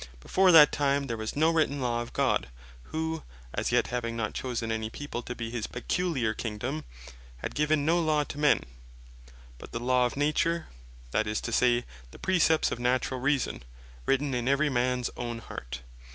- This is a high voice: No, low, 125 Hz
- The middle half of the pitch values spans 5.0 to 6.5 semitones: No, average, 4.3 semitones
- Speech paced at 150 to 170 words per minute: No, average, 180 wpm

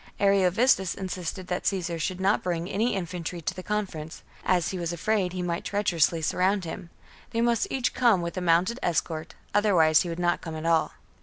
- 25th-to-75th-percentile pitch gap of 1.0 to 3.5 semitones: Yes, average, 2.8 semitones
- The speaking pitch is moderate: Yes, medium, 180 Hz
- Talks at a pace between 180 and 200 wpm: Yes, average, 190 wpm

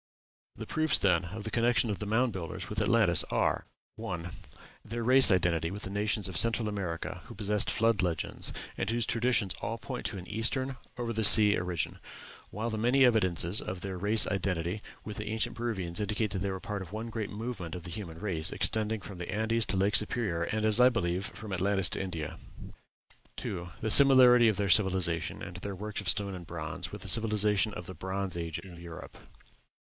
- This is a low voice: Yes, low, 105 Hz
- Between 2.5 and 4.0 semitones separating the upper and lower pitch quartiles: Yes, average, 3.6 semitones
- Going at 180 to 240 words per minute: Yes, average, 200 wpm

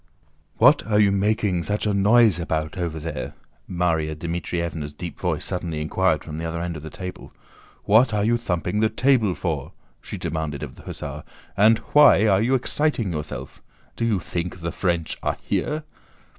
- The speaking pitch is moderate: No, very low, 90 Hz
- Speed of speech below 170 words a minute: No, average, 175 wpm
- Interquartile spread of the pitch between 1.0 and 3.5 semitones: No, average, 4.6 semitones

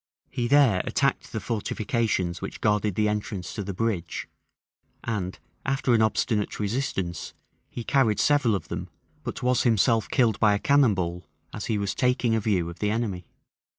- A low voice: Yes, low, 110 Hz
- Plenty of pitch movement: No, average, 3.3 semitones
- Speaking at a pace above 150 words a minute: Yes, average, 170 wpm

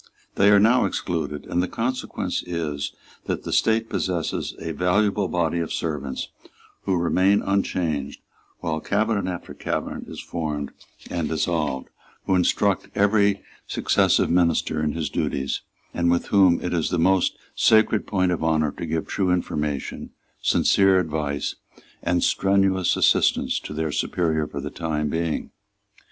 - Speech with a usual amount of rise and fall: Yes, average, 3.6 semitones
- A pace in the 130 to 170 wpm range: Yes, average, 145 wpm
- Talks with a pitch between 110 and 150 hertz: No, very low, 85 Hz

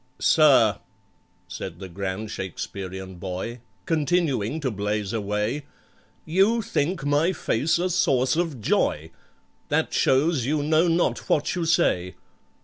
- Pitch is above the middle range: No, low, 130 Hz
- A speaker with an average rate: No, slow, 125 wpm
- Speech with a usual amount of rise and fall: No, wide, 8.3 semitones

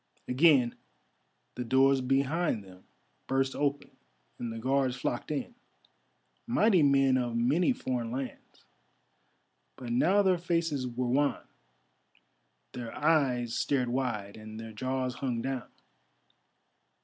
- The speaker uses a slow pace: Yes, slow, 115 wpm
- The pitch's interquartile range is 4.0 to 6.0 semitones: No, average, 3.0 semitones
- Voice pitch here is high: No, low, 130 Hz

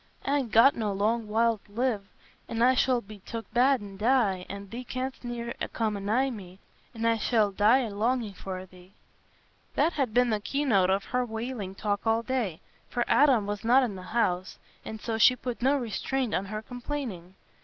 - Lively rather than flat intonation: No, average, 3.7 semitones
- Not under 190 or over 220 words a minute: Yes, average, 200 wpm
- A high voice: Yes, high, 225 Hz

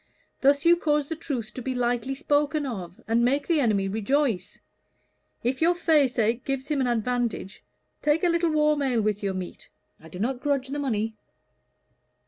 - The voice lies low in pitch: No, very high, 260 Hz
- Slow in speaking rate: No, average, 175 wpm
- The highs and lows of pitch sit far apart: No, average, 4.8 semitones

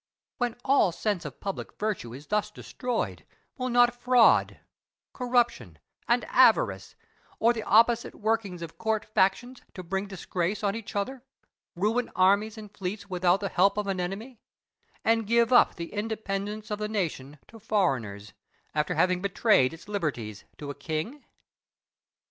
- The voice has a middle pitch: No, high, 205 Hz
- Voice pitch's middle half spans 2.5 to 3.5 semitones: No, average, 4.1 semitones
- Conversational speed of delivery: Yes, average, 150 wpm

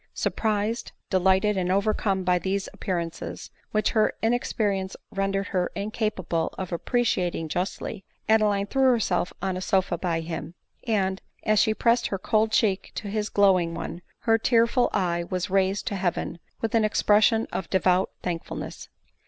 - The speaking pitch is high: Yes, high, 195 Hz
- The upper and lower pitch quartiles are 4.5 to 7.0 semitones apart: No, average, 2.8 semitones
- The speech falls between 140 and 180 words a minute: Yes, average, 150 wpm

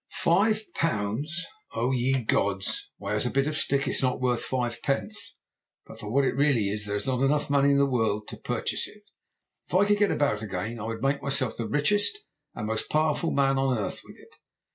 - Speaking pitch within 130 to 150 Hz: Yes, low, 135 Hz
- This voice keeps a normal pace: No, fast, 215 wpm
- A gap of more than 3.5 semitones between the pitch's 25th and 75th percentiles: Yes, average, 4.6 semitones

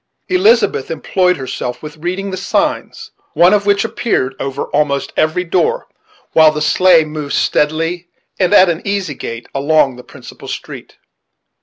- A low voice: No, medium, 165 Hz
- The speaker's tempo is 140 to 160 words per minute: Yes, average, 150 wpm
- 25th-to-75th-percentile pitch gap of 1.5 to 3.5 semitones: No, average, 4.3 semitones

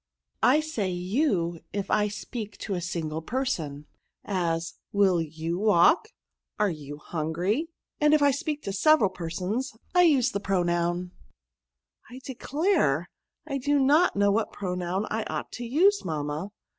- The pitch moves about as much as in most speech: No, wide, 7.5 semitones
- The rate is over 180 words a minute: No, average, 160 wpm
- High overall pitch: Yes, high, 200 Hz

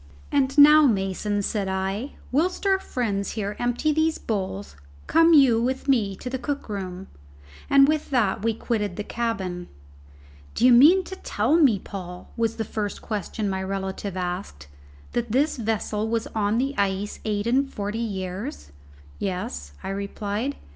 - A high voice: Yes, high, 215 Hz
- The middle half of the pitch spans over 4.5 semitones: Yes, average, 5.1 semitones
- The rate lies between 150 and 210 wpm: Yes, average, 155 wpm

